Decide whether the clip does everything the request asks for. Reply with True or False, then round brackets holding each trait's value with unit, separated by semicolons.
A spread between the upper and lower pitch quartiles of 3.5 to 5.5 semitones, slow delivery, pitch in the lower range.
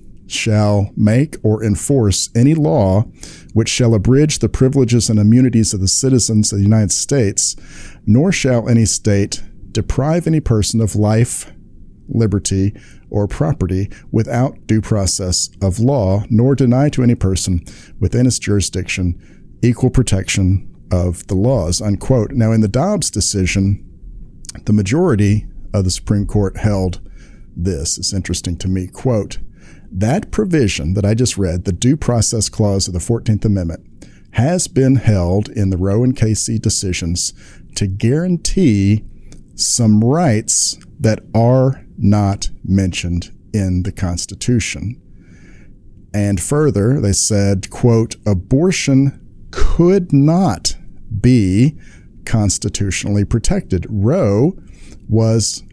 True (3.9 semitones; 125 wpm; 105 Hz)